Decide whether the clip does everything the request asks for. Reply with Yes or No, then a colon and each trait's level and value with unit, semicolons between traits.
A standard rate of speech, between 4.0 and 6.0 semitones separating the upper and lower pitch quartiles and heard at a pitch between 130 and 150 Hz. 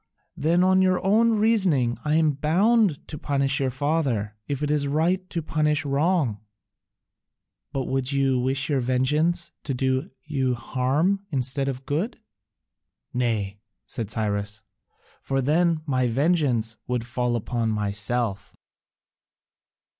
No: slow, 130 wpm; average, 4.6 semitones; medium, 140 Hz